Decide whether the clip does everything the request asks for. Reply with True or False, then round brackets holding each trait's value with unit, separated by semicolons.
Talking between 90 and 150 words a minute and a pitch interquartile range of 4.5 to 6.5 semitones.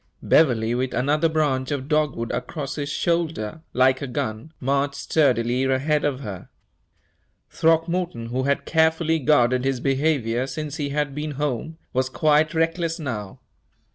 False (140 wpm; 3.5 semitones)